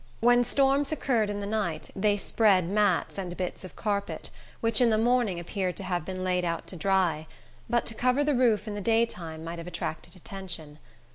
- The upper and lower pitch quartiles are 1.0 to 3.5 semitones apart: No, average, 4.3 semitones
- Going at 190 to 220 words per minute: Yes, average, 200 wpm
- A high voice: Yes, high, 200 Hz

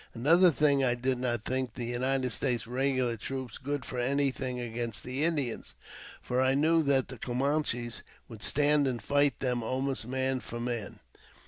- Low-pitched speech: Yes, low, 130 Hz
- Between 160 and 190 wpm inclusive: Yes, average, 165 wpm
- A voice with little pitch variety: Yes, narrow, 2.3 semitones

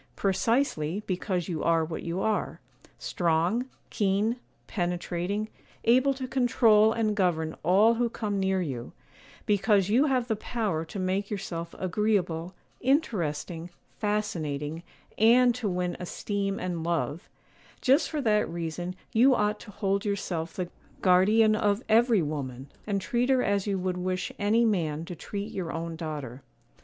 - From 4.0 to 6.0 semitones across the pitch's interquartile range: Yes, average, 4.4 semitones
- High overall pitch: Yes, high, 195 Hz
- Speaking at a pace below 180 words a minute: Yes, average, 140 wpm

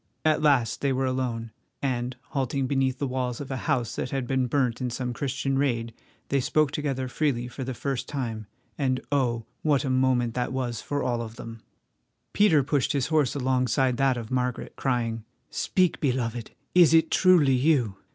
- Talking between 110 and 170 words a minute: No, average, 180 wpm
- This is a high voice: No, low, 130 Hz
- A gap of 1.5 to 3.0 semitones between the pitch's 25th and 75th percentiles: Yes, narrow, 2.4 semitones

